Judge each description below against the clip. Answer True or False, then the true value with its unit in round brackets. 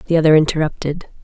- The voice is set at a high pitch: False (155 Hz)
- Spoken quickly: False (145 wpm)